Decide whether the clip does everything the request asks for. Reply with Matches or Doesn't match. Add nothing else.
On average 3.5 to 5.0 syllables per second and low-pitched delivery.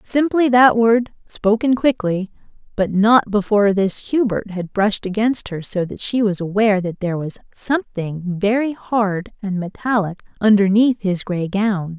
Doesn't match